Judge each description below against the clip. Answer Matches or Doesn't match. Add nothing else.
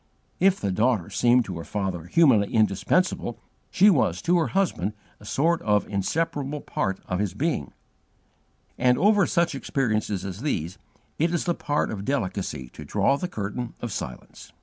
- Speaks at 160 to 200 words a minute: Matches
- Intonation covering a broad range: Matches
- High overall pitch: Doesn't match